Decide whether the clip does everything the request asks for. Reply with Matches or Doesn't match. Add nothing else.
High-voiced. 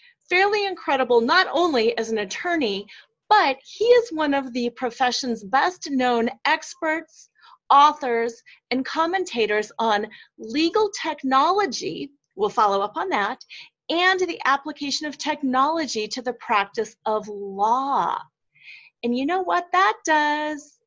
Matches